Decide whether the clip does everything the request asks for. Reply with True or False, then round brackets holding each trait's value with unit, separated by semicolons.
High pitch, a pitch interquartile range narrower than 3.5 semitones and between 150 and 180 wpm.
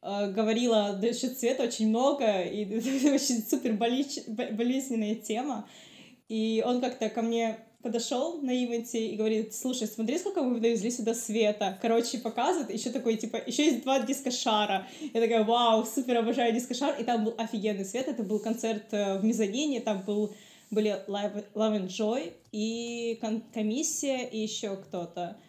True (230 Hz; 2.4 semitones; 155 wpm)